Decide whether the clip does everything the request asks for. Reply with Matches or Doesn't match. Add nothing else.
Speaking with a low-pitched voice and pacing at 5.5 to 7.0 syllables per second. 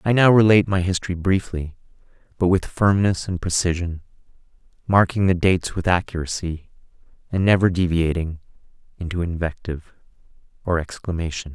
Matches